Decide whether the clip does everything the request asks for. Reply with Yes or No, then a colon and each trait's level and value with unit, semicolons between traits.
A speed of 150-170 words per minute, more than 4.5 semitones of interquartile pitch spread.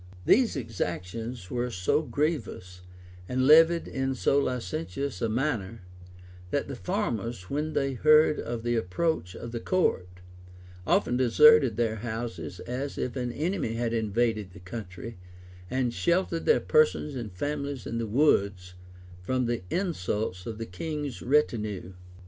No: average, 140 wpm; average, 5.3 semitones